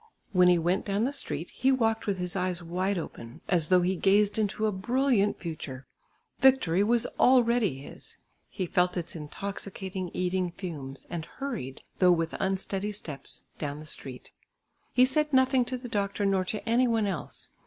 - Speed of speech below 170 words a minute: No, average, 175 wpm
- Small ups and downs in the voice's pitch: No, average, 4.5 semitones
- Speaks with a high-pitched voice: Yes, high, 195 Hz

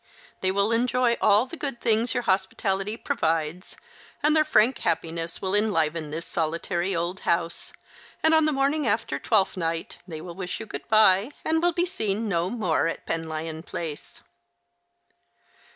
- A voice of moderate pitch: No, high, 195 Hz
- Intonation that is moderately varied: No, wide, 6.0 semitones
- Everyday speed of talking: Yes, average, 160 wpm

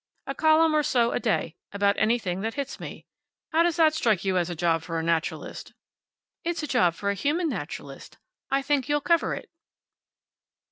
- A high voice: Yes, high, 245 Hz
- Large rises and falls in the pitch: Yes, wide, 8.7 semitones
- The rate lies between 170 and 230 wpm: Yes, average, 190 wpm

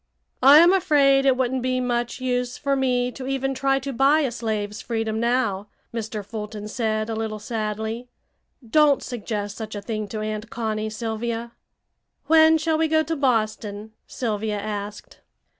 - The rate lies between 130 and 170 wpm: Yes, average, 160 wpm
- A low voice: No, high, 235 Hz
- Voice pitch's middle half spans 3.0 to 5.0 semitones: Yes, average, 3.8 semitones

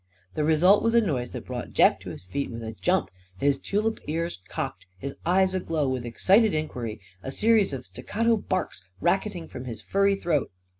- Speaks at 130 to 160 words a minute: No, average, 190 wpm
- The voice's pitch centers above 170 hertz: No, medium, 160 Hz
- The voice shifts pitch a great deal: Yes, wide, 7.4 semitones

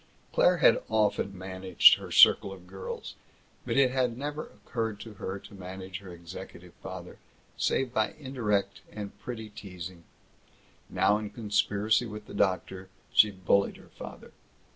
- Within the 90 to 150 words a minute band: Yes, average, 145 wpm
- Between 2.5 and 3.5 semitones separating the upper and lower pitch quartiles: Yes, average, 2.8 semitones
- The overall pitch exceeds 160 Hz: No, low, 105 Hz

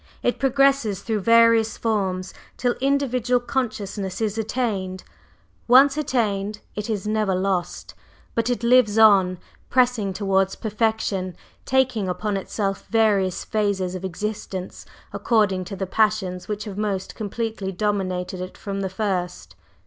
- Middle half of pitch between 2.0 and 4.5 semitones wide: Yes, average, 3.2 semitones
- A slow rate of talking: Yes, slow, 130 wpm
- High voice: Yes, high, 210 Hz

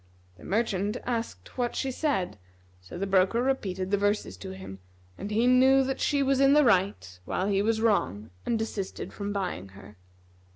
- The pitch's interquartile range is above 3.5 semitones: Yes, average, 4.8 semitones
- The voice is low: No, high, 205 Hz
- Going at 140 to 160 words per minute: No, average, 180 wpm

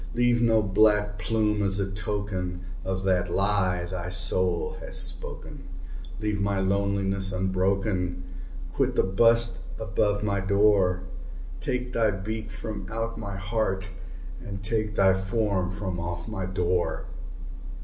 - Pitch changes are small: Yes, narrow, 2.2 semitones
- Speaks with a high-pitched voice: No, low, 100 Hz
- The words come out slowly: Yes, slow, 130 wpm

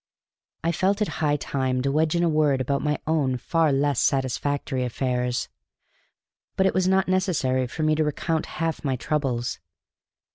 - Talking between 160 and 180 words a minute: Yes, average, 170 wpm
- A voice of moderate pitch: Yes, medium, 145 Hz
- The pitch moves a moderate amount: Yes, average, 3.7 semitones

